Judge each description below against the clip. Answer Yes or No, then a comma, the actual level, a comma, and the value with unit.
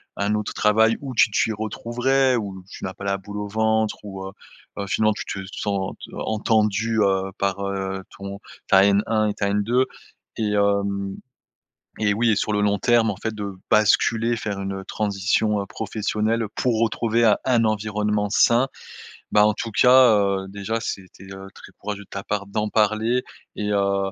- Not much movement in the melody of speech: Yes, narrow, 2.0 semitones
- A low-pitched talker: Yes, low, 105 Hz